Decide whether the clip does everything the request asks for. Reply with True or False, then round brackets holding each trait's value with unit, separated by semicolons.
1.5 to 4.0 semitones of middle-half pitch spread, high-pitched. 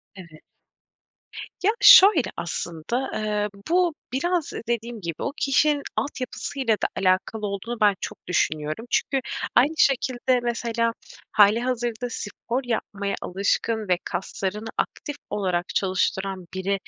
False (4.8 semitones; 225 Hz)